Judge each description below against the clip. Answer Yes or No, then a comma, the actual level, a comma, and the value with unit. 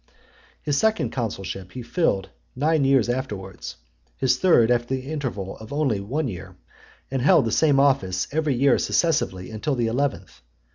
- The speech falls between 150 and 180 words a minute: Yes, average, 155 wpm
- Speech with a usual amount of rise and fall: No, wide, 6.2 semitones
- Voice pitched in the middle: No, low, 130 Hz